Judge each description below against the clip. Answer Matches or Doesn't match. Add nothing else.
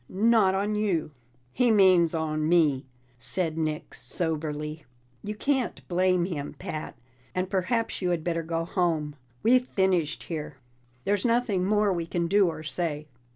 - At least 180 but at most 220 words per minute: Doesn't match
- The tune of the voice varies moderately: Matches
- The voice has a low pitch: Doesn't match